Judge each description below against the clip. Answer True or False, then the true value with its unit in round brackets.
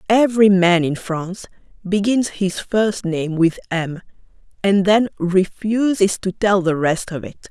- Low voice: False (190 Hz)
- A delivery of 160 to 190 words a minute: False (150 wpm)